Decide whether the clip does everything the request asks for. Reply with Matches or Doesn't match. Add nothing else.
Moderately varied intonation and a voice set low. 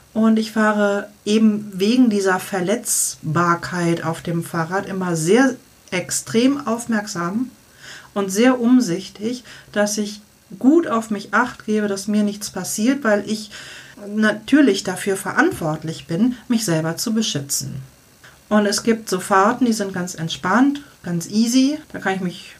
Doesn't match